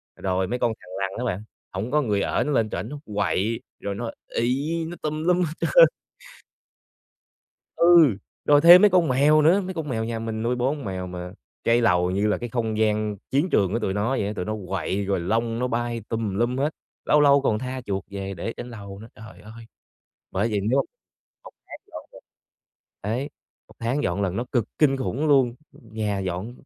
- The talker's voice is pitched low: Yes, low, 115 Hz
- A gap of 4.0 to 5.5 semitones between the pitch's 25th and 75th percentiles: Yes, average, 5.2 semitones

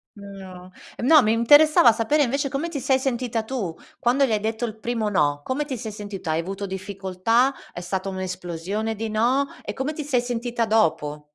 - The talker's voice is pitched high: Yes, high, 220 Hz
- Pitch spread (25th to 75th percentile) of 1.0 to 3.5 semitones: No, average, 5.1 semitones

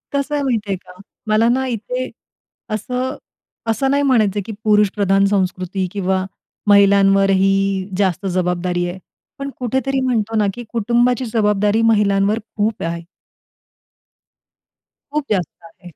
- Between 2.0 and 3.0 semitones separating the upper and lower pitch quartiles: No, average, 3.7 semitones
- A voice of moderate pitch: No, high, 205 Hz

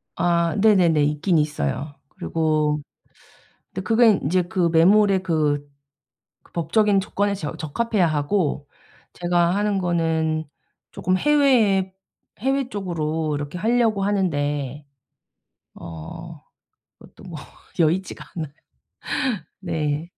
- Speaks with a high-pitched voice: No, medium, 170 Hz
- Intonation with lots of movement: No, average, 4.5 semitones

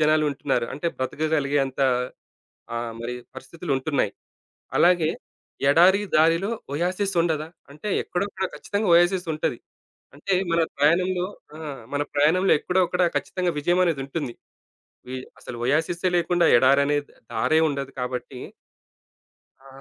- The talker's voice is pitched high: No, medium, 155 Hz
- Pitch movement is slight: No, average, 4.1 semitones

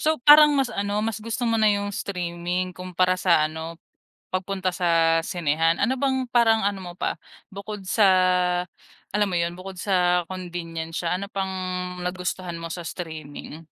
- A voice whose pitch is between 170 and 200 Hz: Yes, medium, 185 Hz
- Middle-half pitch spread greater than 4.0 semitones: No, average, 3.2 semitones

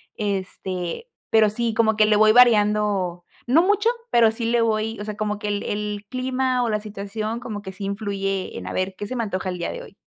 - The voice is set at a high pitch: Yes, high, 210 Hz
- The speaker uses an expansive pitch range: No, narrow, 2.4 semitones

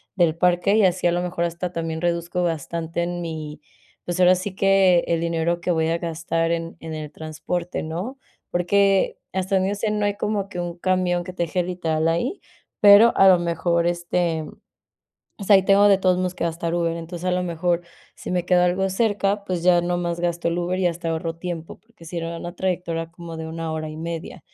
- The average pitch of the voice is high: No, medium, 175 Hz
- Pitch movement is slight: Yes, narrow, 1.8 semitones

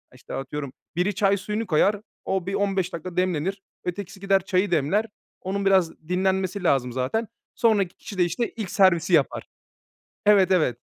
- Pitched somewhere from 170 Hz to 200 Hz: Yes, high, 190 Hz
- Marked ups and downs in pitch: No, average, 2.7 semitones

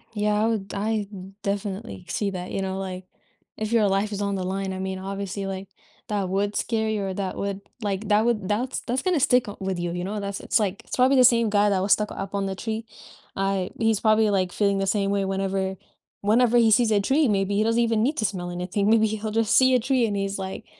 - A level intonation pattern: Yes, narrow, 2.2 semitones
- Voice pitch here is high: Yes, high, 205 Hz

